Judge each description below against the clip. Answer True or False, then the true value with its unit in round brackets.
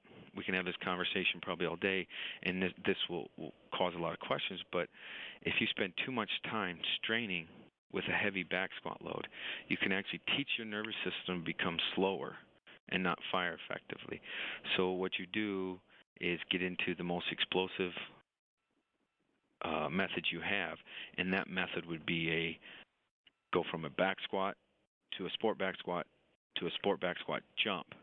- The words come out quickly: False (175 wpm)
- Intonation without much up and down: True (1.7 semitones)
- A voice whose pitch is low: True (90 Hz)